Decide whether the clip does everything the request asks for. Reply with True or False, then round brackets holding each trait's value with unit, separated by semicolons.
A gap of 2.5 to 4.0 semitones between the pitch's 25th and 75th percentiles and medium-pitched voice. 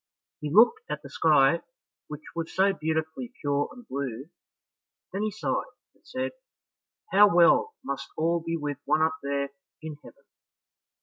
False (5.2 semitones; 160 Hz)